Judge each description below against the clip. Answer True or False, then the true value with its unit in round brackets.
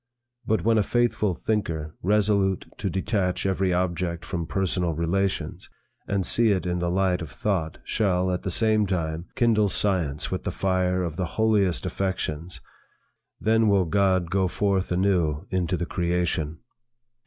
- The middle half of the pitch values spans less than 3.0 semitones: True (2.4 semitones)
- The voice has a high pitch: False (95 Hz)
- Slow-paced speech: False (155 wpm)